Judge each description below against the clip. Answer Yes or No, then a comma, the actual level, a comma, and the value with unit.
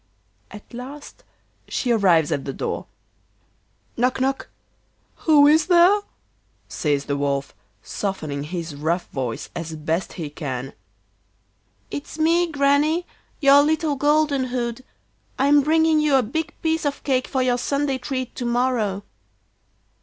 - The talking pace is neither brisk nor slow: No, slow, 130 wpm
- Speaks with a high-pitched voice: Yes, very high, 255 Hz